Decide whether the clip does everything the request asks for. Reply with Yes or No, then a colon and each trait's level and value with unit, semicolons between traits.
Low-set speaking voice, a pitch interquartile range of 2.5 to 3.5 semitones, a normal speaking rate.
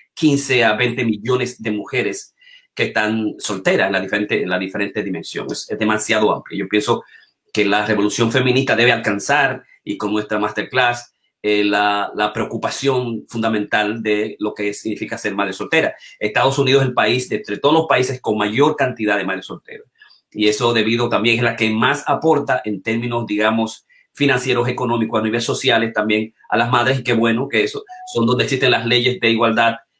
Yes: low, 115 Hz; average, 3.1 semitones; average, 180 wpm